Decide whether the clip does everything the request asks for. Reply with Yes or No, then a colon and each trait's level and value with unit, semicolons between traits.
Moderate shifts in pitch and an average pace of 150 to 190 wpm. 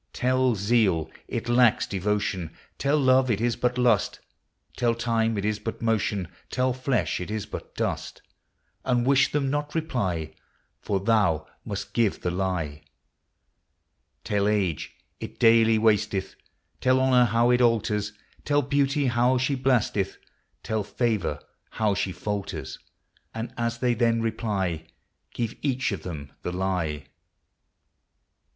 No: average, 4.0 semitones; slow, 135 wpm